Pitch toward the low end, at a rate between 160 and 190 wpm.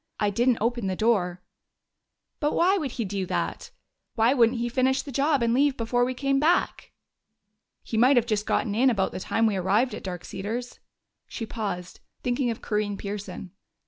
No: high, 230 Hz; average, 185 wpm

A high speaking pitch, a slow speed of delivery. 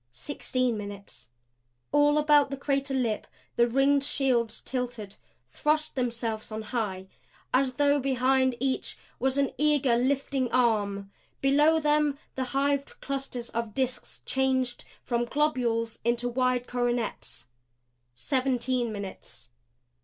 Yes: very high, 255 Hz; slow, 115 wpm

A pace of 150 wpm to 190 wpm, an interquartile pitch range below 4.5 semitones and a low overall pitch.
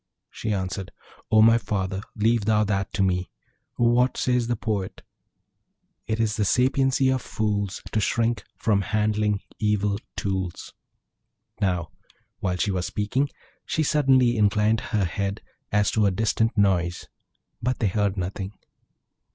No: average, 140 wpm; average, 2.7 semitones; low, 105 Hz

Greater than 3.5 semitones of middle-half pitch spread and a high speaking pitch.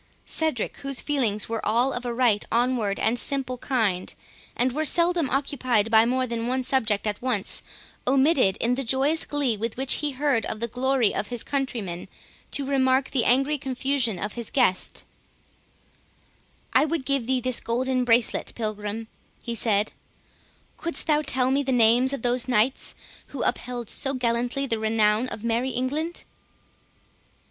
No: average, 3.1 semitones; very high, 250 Hz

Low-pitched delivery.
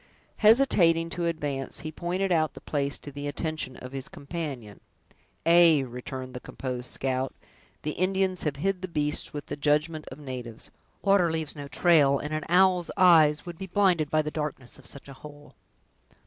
No: medium, 150 Hz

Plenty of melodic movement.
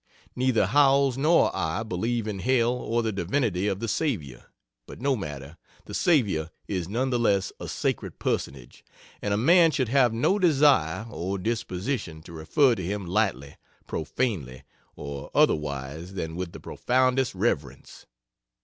Yes: wide, 7.4 semitones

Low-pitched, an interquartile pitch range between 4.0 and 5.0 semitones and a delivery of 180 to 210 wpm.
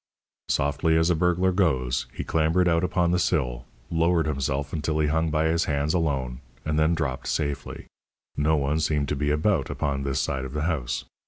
No: very low, 75 Hz; average, 3.0 semitones; average, 190 wpm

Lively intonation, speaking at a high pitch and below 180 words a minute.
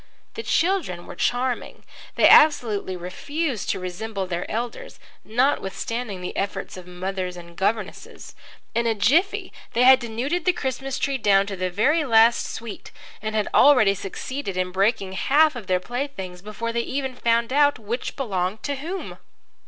Yes: wide, 5.7 semitones; high, 225 Hz; average, 160 wpm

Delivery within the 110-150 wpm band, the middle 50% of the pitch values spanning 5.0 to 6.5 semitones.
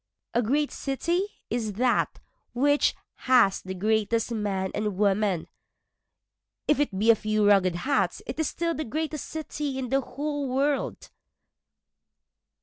Yes: average, 140 wpm; wide, 5.6 semitones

